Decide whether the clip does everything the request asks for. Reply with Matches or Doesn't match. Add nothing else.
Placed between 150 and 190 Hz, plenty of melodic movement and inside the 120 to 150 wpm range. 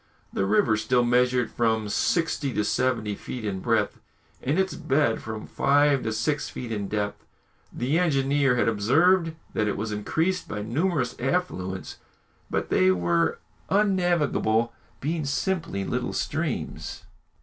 Doesn't match